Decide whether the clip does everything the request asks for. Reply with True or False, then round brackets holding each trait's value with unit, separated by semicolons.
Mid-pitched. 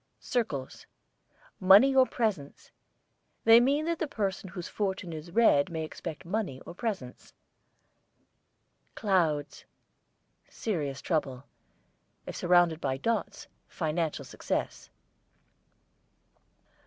True (180 Hz)